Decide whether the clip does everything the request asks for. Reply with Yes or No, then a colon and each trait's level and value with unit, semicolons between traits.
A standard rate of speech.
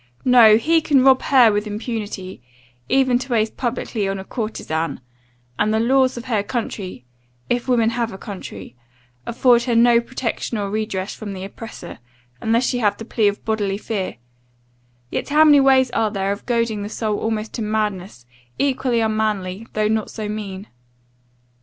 Yes: average, 170 wpm